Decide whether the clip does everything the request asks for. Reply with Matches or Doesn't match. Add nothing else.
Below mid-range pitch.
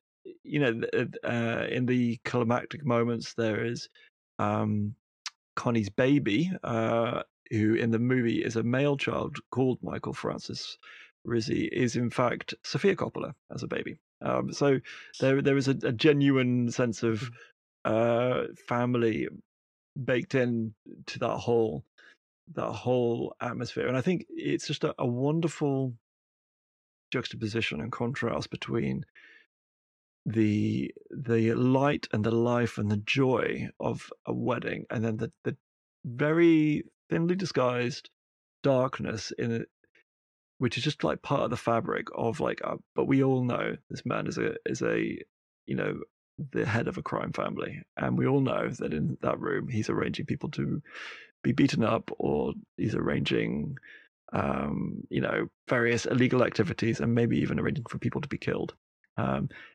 Matches